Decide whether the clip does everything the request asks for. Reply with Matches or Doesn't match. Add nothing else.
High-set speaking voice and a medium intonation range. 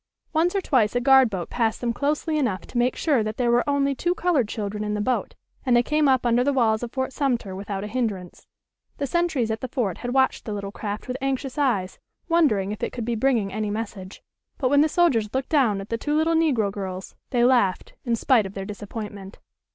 Matches